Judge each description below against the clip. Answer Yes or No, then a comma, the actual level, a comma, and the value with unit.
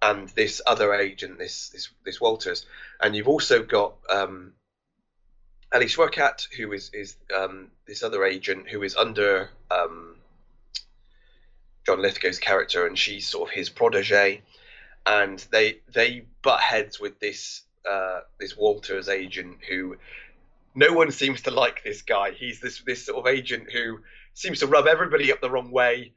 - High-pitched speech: No, low, 125 Hz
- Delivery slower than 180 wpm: Yes, average, 160 wpm